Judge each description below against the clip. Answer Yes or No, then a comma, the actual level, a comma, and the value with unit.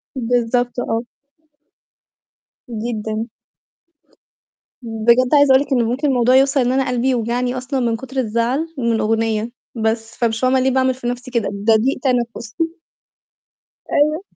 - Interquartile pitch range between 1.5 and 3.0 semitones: Yes, narrow, 2.4 semitones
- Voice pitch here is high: Yes, high, 245 Hz